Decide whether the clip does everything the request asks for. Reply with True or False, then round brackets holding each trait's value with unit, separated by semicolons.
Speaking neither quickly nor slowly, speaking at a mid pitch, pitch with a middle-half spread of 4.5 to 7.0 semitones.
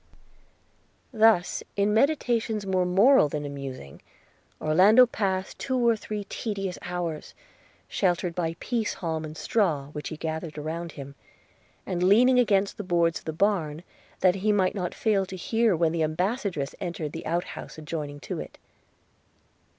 True (150 wpm; 180 Hz; 4.8 semitones)